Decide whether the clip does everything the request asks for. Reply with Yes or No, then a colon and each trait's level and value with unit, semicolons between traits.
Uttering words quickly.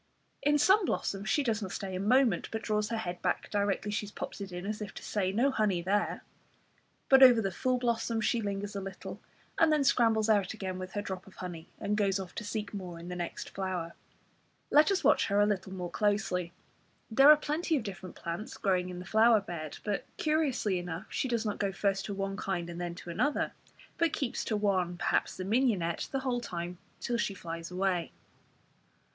Yes: fast, 215 wpm